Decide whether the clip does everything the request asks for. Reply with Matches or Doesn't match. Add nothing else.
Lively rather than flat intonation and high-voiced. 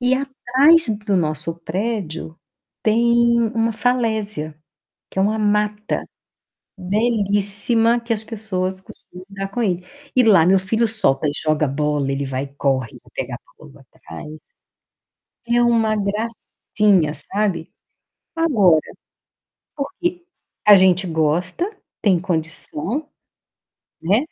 Matches